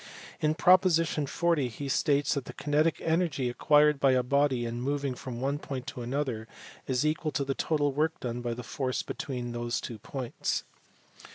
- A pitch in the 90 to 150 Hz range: Yes, medium, 140 Hz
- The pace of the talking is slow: No, average, 185 wpm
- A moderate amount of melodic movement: Yes, average, 3.3 semitones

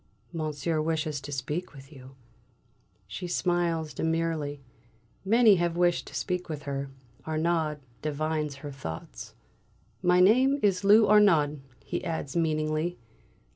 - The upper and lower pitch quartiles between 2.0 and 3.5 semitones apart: Yes, average, 3.2 semitones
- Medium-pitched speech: Yes, medium, 160 Hz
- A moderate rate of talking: No, slow, 125 wpm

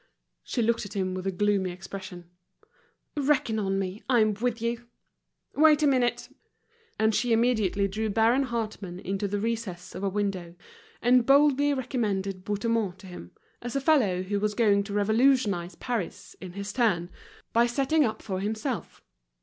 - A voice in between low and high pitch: No, high, 215 Hz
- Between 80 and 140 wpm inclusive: No, average, 160 wpm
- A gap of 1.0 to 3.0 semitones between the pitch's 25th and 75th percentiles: No, average, 3.8 semitones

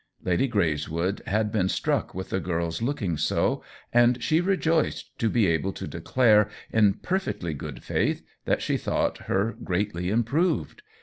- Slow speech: No, average, 150 wpm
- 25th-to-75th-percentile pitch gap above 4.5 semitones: Yes, wide, 5.4 semitones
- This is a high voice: No, low, 105 Hz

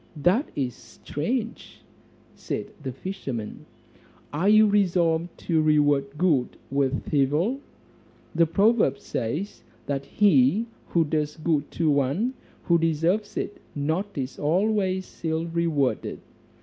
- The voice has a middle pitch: Yes, medium, 160 Hz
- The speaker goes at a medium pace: No, slow, 115 wpm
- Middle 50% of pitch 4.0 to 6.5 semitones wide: Yes, average, 5.1 semitones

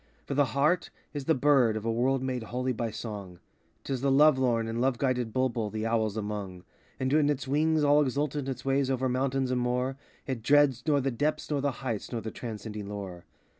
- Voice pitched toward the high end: No, low, 130 Hz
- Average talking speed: No, fast, 215 wpm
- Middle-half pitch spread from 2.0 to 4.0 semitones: Yes, average, 3.6 semitones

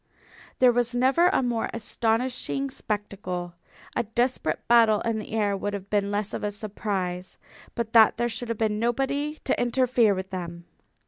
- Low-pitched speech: No, high, 225 Hz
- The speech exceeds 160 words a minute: Yes, average, 170 wpm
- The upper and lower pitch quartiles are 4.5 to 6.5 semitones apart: No, average, 3.1 semitones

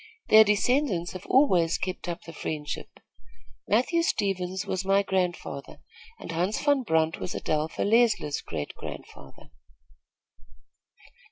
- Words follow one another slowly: Yes, slow, 115 wpm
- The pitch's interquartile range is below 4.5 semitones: No, average, 4.8 semitones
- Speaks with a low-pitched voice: No, medium, 185 Hz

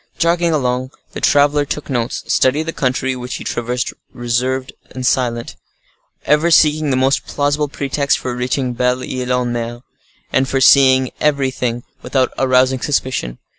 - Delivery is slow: No, average, 150 wpm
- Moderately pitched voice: No, low, 130 Hz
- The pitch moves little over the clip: Yes, narrow, 2.3 semitones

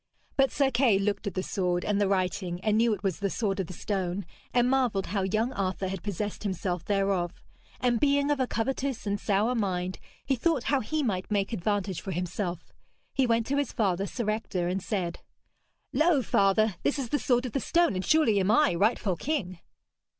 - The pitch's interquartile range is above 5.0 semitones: No, average, 4.7 semitones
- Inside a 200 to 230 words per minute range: Yes, fast, 205 wpm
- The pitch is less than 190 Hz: No, high, 205 Hz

